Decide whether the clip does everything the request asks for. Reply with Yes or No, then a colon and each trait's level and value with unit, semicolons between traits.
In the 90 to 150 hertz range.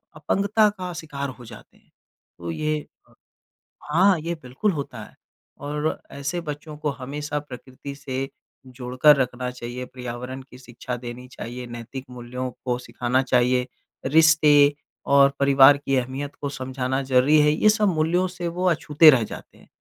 Yes: low, 135 Hz